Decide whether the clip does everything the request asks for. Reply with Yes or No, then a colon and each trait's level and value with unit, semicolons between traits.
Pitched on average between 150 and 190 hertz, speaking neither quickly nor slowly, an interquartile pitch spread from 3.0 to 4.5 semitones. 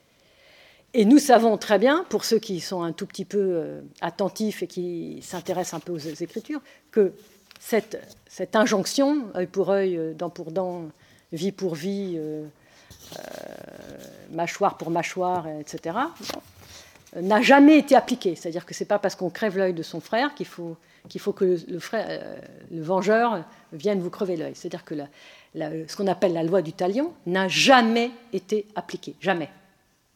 Yes: medium, 185 Hz; average, 170 wpm; average, 3.7 semitones